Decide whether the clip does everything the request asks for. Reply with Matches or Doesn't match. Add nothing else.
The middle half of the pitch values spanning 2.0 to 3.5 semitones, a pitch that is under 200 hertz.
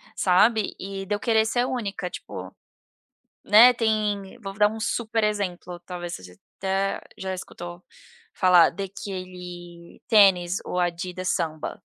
Matches